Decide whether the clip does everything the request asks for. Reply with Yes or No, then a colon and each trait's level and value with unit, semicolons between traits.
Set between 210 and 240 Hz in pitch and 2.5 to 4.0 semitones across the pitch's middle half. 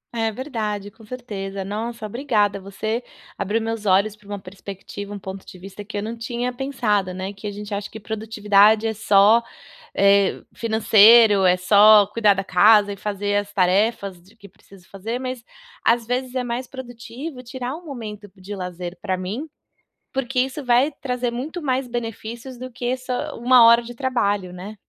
Yes: high, 215 Hz; average, 3.3 semitones